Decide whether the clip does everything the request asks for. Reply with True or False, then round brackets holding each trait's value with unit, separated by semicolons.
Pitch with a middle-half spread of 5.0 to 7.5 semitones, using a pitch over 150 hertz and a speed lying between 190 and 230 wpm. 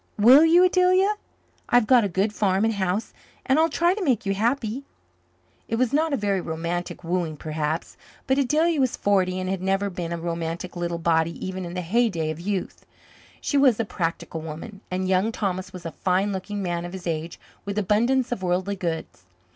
True (5.4 semitones; 190 Hz; 195 wpm)